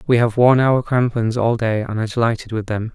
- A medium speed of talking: No, fast, 245 wpm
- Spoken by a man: Yes, male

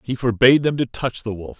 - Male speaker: Yes, male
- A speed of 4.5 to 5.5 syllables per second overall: No, 6.0 syllables/s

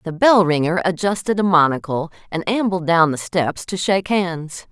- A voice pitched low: No, medium, 175 Hz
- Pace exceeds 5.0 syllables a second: No, 4.9 syllables/s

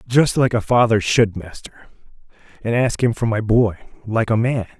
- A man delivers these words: Yes, male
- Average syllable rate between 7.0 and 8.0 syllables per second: No, 4.9 syllables/s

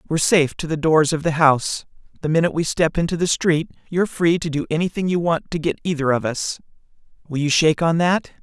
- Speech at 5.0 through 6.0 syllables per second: No, 6.3 syllables/s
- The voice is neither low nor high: Yes, medium, 160 Hz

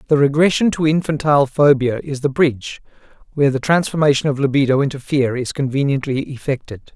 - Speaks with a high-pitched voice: No, medium, 140 Hz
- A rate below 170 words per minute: Yes, average, 155 wpm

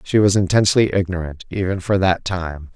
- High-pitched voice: No, very low, 95 Hz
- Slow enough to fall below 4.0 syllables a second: No, 5.5 syllables/s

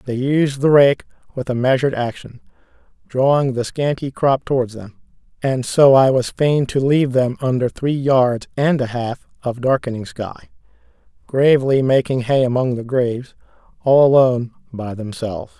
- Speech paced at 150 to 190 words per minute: Yes, average, 160 wpm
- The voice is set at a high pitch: No, low, 130 Hz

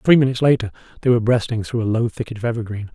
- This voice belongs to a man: Yes, male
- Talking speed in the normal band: No, fast, 245 wpm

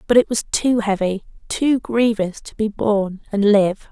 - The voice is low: No, high, 210 Hz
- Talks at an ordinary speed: Yes, average, 185 wpm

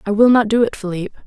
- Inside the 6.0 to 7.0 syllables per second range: Yes, 6.8 syllables/s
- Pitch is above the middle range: Yes, high, 215 Hz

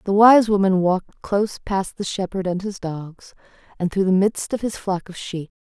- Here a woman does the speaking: Yes, female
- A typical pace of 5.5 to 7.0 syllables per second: No, 4.9 syllables/s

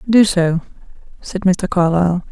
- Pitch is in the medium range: Yes, medium, 180 Hz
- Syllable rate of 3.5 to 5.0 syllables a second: Yes, 4.7 syllables/s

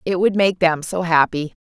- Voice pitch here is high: No, medium, 175 Hz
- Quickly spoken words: Yes, fast, 220 wpm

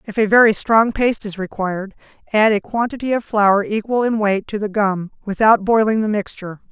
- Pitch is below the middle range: No, high, 210 Hz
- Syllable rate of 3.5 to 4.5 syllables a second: No, 5.5 syllables/s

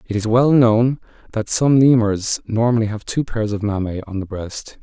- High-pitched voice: No, low, 110 Hz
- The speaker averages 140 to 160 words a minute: No, average, 200 wpm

